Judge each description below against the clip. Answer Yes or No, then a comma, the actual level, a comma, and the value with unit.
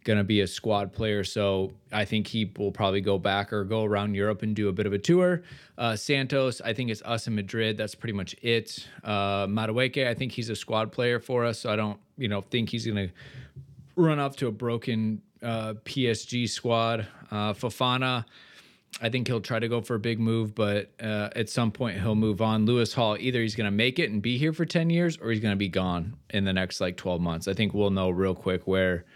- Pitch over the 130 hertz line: No, low, 110 Hz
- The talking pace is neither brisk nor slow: No, fast, 235 wpm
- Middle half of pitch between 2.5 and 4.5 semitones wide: Yes, average, 2.9 semitones